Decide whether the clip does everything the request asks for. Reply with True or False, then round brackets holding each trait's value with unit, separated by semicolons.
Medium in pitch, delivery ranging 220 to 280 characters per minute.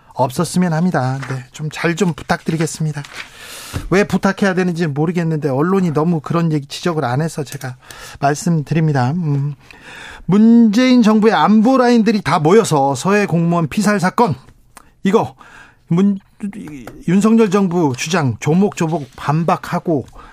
False (170 Hz; 295 characters per minute)